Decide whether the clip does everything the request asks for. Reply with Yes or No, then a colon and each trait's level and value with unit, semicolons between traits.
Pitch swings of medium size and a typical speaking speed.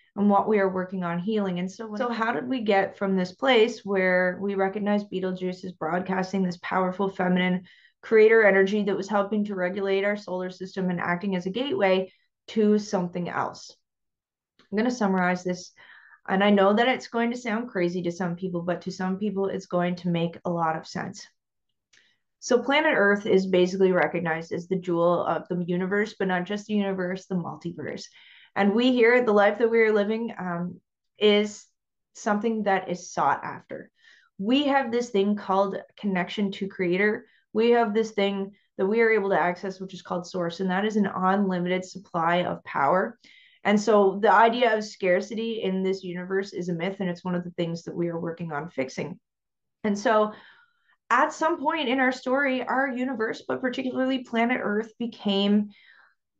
Yes: average, 3.4 semitones; average, 190 wpm